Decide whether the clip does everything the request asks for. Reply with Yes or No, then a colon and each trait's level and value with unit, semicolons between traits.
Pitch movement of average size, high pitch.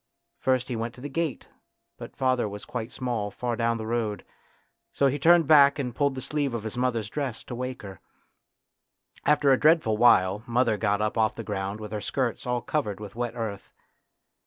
No: average, 3.7 semitones; low, 120 Hz